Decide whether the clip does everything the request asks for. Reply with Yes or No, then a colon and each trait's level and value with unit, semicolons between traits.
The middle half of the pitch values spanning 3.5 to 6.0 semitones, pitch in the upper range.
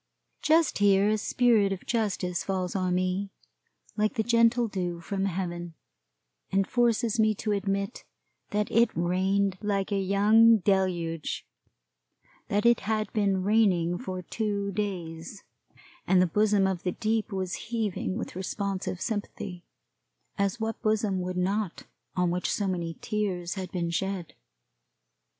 No: average, 2.8 semitones; high, 195 Hz